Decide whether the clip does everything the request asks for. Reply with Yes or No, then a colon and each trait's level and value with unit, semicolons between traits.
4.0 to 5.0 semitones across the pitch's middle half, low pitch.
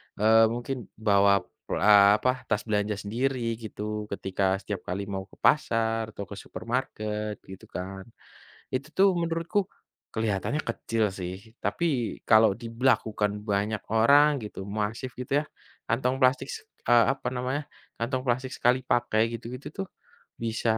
No: average, 3.6 semitones; low, 115 Hz